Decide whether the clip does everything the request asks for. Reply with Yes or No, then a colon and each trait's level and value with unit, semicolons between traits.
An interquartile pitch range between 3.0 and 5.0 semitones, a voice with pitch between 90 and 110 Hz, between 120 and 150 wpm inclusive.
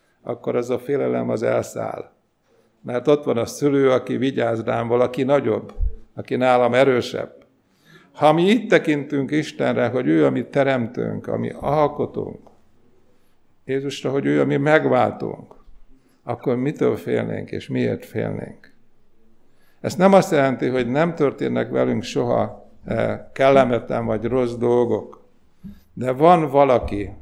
No: average, 3.5 semitones; low, 130 Hz; average, 130 wpm